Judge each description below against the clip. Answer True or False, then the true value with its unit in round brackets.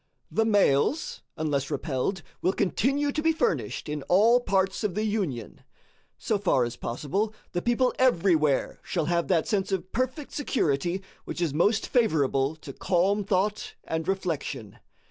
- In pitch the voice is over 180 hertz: True (190 Hz)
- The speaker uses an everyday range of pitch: False (6.2 semitones)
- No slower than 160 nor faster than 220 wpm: False (150 wpm)